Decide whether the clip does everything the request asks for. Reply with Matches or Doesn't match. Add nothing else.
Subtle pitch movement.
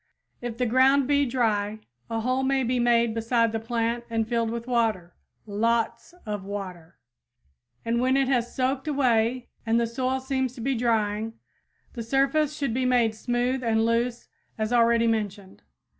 Matches